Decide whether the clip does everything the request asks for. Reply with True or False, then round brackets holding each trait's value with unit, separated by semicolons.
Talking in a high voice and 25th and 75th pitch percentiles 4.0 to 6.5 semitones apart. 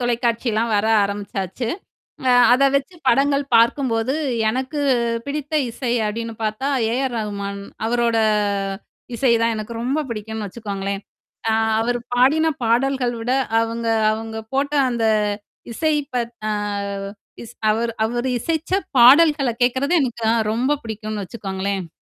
False (235 Hz; 3.2 semitones)